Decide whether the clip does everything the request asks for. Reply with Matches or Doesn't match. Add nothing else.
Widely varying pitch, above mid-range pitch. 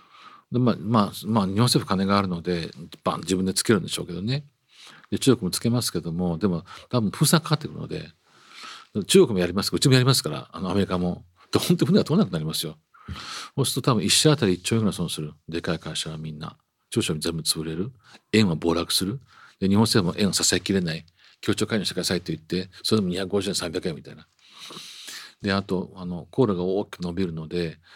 Doesn't match